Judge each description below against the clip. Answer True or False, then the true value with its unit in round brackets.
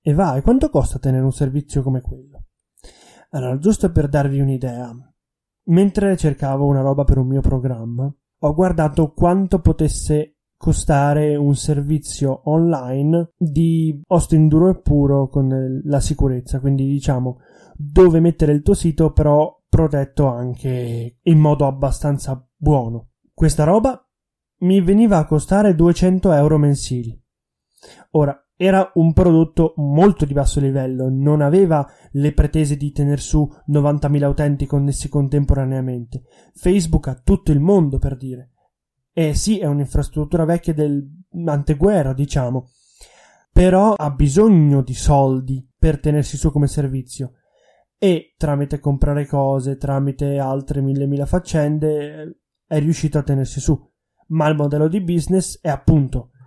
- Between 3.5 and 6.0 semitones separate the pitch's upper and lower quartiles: False (3.0 semitones)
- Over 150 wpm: False (135 wpm)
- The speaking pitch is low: False (145 Hz)